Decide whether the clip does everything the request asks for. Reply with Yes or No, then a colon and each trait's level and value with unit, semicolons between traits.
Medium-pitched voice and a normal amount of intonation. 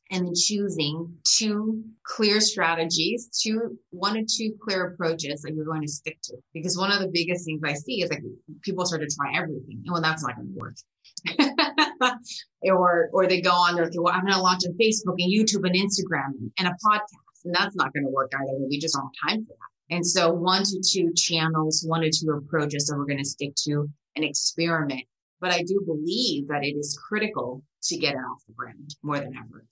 Yes: medium, 170 Hz; average, 4.4 semitones